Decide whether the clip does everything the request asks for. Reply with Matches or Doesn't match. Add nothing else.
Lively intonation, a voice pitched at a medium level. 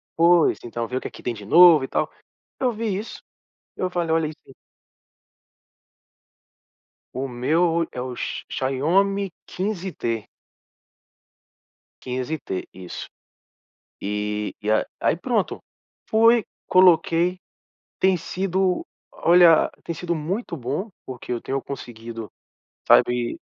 Matches